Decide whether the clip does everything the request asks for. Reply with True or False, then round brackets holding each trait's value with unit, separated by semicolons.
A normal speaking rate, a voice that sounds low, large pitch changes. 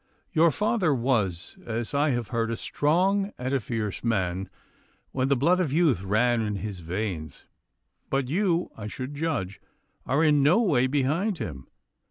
True (165 wpm; 130 Hz; 6.6 semitones)